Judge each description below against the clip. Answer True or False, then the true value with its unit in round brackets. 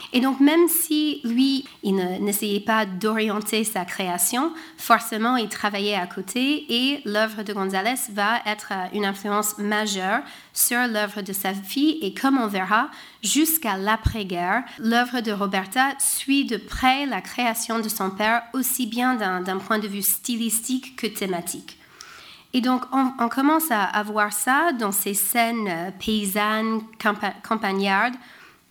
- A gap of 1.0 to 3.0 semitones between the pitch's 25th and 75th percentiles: False (3.7 semitones)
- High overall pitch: True (220 Hz)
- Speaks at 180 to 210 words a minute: False (155 wpm)